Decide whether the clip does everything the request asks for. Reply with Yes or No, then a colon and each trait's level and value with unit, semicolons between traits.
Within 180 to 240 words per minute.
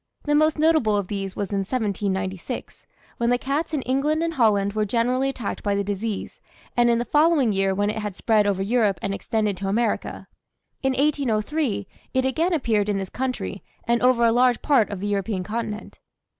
Yes: average, 195 wpm